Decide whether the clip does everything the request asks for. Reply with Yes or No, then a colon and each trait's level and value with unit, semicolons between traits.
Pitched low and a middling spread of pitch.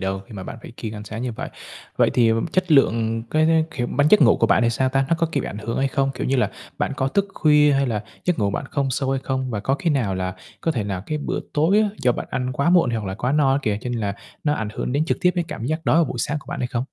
Yes: low, 130 Hz; average, 4.9 semitones